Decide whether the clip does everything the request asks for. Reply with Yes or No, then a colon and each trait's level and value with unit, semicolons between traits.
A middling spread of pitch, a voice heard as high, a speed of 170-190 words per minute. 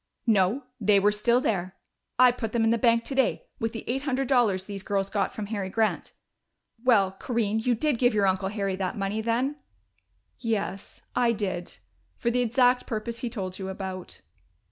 Yes: average, 3.6 semitones; high, 220 Hz; average, 185 wpm